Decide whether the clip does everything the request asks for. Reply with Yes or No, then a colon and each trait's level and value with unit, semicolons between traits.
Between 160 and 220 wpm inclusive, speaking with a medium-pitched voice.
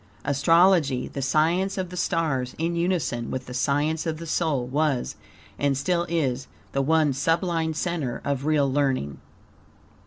No: average, 150 wpm; medium, 155 Hz